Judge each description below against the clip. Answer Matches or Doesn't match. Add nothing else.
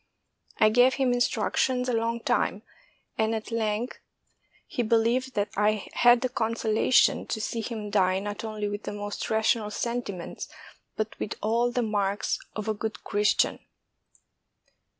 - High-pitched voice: Matches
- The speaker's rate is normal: Matches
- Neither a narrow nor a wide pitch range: Doesn't match